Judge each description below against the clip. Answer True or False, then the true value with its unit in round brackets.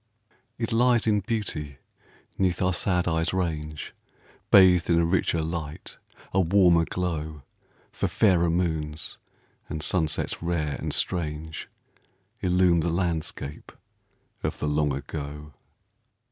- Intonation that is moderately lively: True (3.0 semitones)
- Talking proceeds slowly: True (120 wpm)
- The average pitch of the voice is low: True (85 Hz)